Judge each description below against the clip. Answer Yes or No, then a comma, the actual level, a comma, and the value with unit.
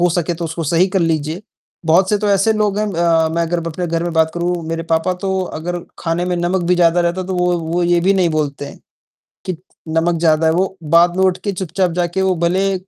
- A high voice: No, medium, 175 Hz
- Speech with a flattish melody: Yes, narrow, 2.0 semitones